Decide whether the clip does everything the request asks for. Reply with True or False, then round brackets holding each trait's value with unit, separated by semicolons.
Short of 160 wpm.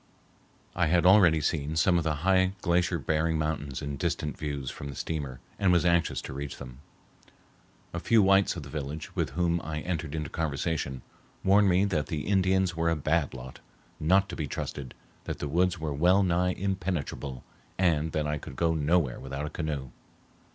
False (185 wpm)